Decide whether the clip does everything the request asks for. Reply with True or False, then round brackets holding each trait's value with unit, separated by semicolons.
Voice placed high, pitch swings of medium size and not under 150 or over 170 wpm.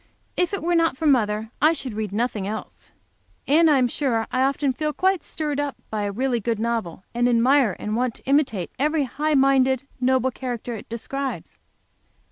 False (260 Hz; 4.1 semitones; 190 wpm)